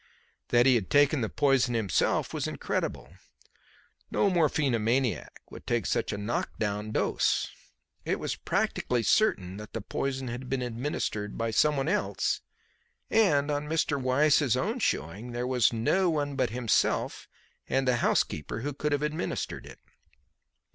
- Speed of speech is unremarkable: Yes, average, 150 wpm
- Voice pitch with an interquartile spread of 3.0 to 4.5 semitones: Yes, average, 4.2 semitones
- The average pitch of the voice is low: Yes, low, 130 Hz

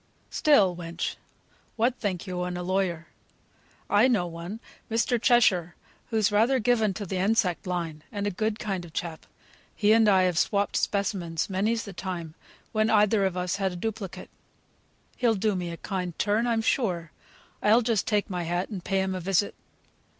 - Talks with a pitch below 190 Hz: No, high, 195 Hz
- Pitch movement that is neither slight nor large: Yes, average, 3.5 semitones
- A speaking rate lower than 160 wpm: No, average, 180 wpm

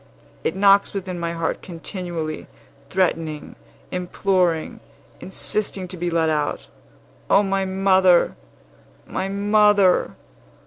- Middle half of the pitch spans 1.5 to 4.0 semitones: Yes, narrow, 2.5 semitones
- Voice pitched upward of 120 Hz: Yes, medium, 185 Hz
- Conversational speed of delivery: No, slow, 100 wpm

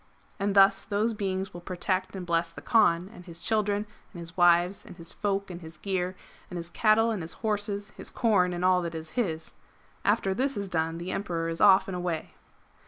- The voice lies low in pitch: No, medium, 185 Hz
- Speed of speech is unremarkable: No, fast, 210 wpm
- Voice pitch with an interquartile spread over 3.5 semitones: No, average, 3.0 semitones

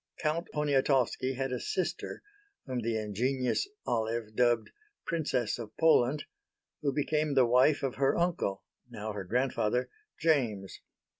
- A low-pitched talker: Yes, low, 130 Hz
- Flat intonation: No, average, 4.0 semitones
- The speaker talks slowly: Yes, slow, 130 wpm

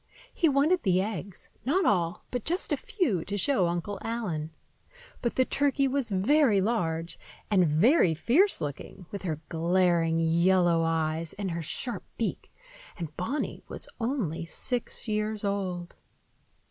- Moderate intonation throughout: No, wide, 6.4 semitones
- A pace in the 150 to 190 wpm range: No, average, 140 wpm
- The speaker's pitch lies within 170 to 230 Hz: Yes, high, 190 Hz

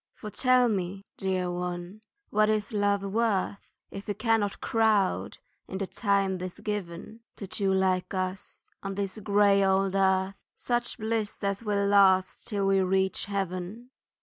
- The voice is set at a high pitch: Yes, high, 195 Hz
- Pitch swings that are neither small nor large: No, narrow, 1.8 semitones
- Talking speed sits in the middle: Yes, average, 150 wpm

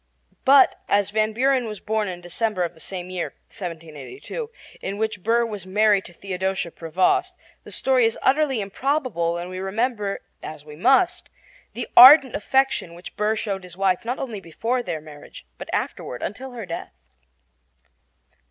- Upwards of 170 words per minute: No, average, 160 wpm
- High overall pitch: Yes, high, 205 Hz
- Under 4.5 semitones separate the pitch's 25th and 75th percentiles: No, wide, 5.5 semitones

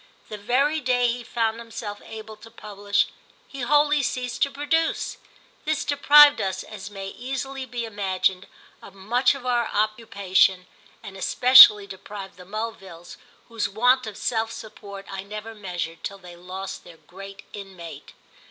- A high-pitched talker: Yes, high, 215 Hz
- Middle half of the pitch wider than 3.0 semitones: Yes, average, 4.2 semitones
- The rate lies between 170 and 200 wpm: No, average, 150 wpm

